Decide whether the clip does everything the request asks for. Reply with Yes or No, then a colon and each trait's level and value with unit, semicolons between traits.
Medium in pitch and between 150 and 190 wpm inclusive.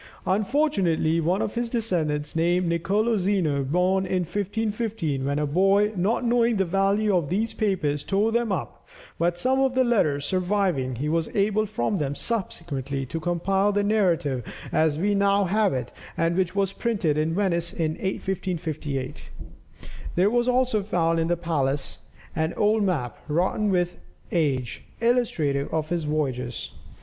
Yes: medium, 180 Hz; average, 155 wpm